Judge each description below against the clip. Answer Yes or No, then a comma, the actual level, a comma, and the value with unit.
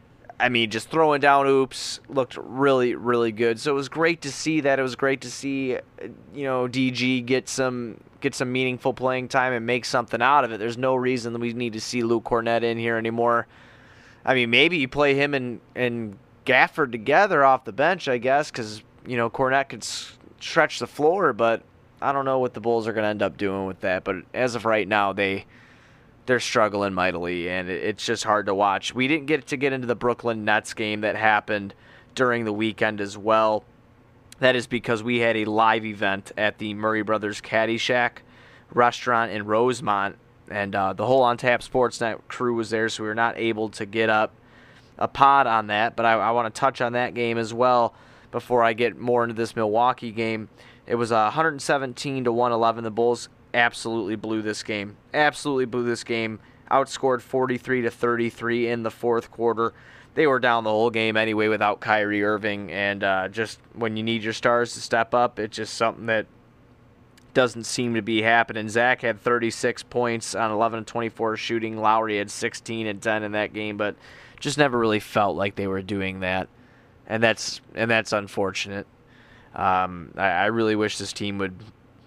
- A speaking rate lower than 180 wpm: No, average, 200 wpm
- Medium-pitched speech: No, low, 115 Hz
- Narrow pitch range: Yes, narrow, 2.3 semitones